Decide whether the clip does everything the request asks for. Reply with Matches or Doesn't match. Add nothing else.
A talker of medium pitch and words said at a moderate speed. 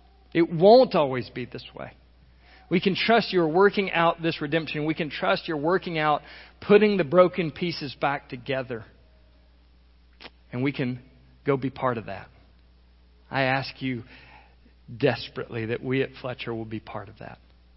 Doesn't match